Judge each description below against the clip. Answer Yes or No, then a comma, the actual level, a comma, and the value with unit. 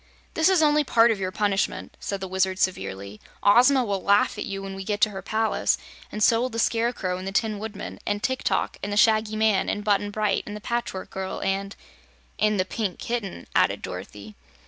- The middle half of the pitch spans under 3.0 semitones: Yes, narrow, 2.6 semitones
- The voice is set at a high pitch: Yes, high, 205 Hz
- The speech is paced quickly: Yes, fast, 215 wpm